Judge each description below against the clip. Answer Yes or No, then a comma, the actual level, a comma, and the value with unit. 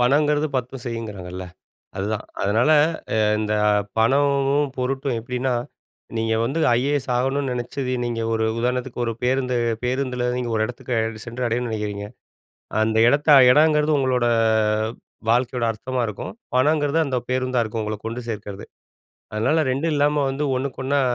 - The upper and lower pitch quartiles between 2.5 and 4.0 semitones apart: Yes, average, 3.4 semitones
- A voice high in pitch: No, low, 125 Hz